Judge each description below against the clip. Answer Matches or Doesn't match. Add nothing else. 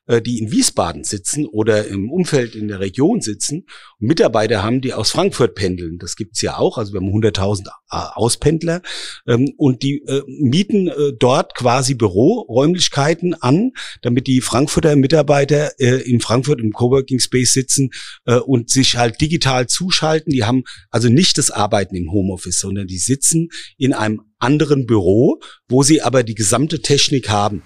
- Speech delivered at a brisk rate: Doesn't match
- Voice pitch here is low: Matches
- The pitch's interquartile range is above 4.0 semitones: Matches